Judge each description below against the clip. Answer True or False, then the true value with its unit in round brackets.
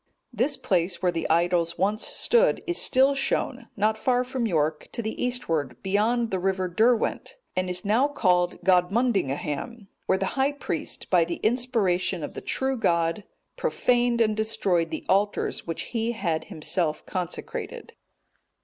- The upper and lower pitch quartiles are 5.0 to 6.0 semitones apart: True (5.4 semitones)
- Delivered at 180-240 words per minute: False (150 wpm)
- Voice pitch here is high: True (200 Hz)